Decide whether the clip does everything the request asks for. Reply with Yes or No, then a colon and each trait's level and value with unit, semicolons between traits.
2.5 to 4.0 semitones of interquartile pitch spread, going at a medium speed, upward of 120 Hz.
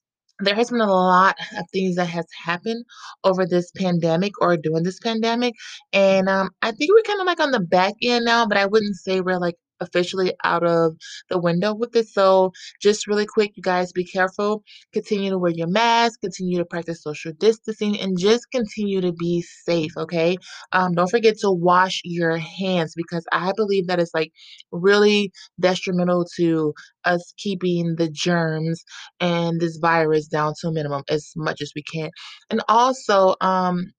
Yes: average, 3.4 semitones; average, 180 wpm; medium, 185 Hz